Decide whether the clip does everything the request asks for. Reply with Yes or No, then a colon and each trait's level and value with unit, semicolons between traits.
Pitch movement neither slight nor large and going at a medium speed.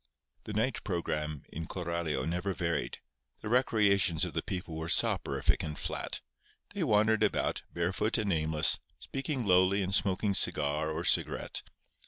Yes: average, 4.6 semitones; average, 145 wpm